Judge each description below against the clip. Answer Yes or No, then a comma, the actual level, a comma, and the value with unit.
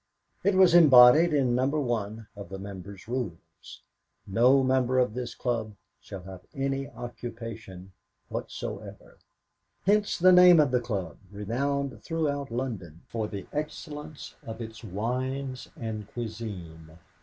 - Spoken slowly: Yes, slow, 130 wpm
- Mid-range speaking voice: No, low, 120 Hz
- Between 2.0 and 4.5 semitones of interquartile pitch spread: No, average, 5.2 semitones